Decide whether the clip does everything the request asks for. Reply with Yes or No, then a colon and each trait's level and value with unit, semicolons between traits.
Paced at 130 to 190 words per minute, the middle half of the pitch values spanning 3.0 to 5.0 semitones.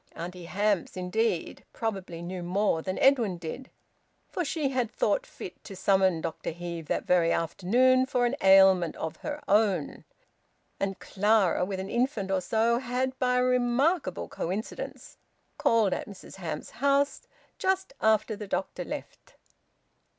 No: average, 145 wpm; wide, 5.6 semitones